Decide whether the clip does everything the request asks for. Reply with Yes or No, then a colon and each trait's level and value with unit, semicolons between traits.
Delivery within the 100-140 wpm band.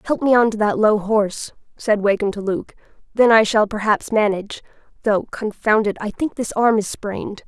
No: average, 185 wpm